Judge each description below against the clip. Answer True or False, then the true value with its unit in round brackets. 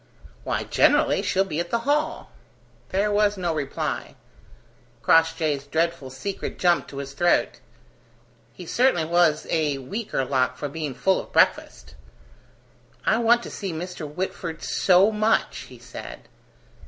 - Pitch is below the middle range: False (170 Hz)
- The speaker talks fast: False (140 wpm)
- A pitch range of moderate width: True (4.8 semitones)